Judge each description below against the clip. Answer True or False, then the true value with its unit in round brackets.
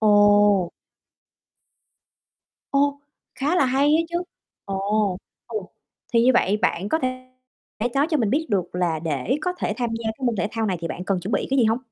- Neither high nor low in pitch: False (220 Hz)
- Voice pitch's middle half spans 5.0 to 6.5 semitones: True (5.3 semitones)